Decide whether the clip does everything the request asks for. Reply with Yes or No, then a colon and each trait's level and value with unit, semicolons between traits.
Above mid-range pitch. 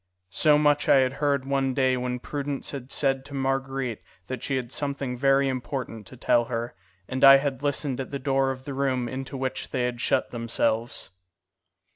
No: low, 135 Hz